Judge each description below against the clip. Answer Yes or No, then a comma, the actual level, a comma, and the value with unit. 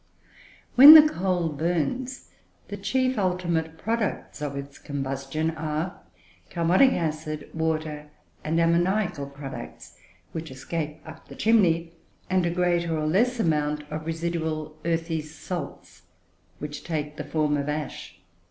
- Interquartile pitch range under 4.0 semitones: Yes, average, 2.8 semitones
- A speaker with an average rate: No, slow, 125 wpm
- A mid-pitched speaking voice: Yes, medium, 160 Hz